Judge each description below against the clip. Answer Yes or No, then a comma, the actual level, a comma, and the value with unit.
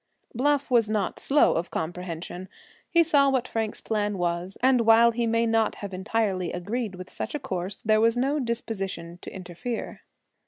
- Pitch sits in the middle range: No, high, 220 Hz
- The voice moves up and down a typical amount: Yes, average, 4.5 semitones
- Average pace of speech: Yes, average, 170 wpm